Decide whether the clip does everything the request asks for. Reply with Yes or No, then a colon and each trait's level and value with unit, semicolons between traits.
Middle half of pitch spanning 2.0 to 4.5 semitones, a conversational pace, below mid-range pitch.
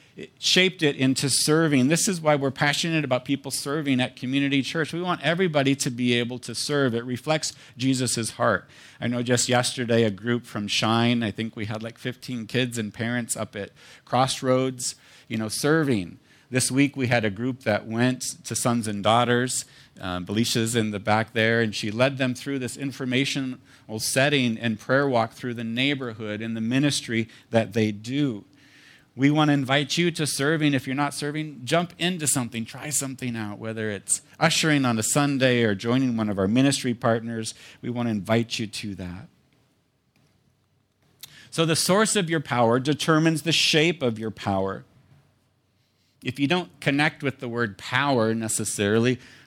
Yes: average, 3.6 semitones; average, 180 wpm; low, 125 Hz